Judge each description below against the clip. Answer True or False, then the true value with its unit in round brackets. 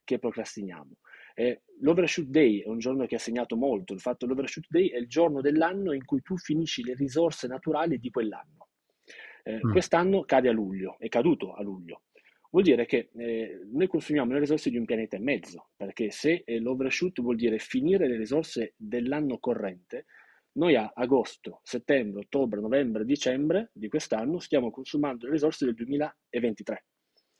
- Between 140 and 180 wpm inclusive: True (165 wpm)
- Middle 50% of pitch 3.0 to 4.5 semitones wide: False (5.6 semitones)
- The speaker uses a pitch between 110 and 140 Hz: True (135 Hz)